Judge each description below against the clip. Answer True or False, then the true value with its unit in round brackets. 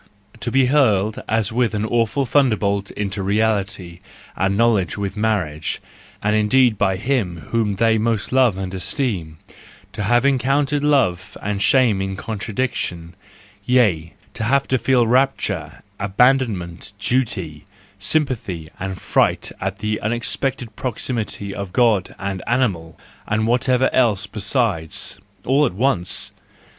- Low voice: True (110 Hz)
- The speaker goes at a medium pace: False (130 wpm)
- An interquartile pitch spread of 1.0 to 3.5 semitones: False (4.5 semitones)